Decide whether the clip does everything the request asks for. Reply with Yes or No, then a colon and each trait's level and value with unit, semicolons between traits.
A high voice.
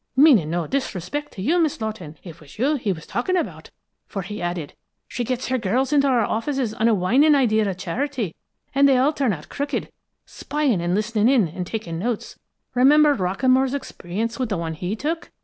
Yes: high, 230 Hz